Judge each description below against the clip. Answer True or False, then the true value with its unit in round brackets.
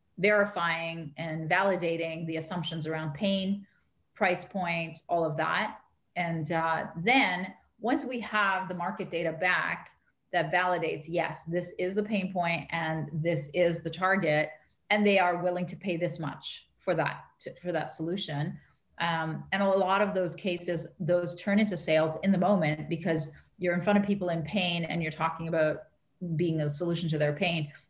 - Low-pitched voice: False (170 Hz)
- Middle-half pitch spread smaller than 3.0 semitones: True (2.4 semitones)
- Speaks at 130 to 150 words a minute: False (175 wpm)